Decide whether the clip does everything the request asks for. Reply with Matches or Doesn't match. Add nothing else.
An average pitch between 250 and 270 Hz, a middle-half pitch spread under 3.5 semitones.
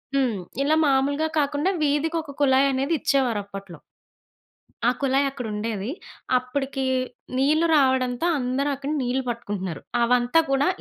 Matches